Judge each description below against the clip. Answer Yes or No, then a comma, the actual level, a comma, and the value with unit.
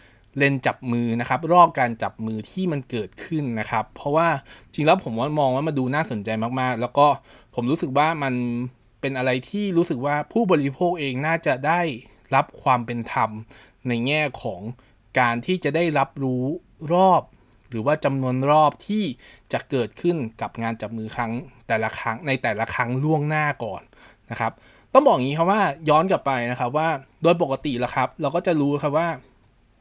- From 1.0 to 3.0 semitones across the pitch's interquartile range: No, average, 4.7 semitones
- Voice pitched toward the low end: Yes, low, 130 Hz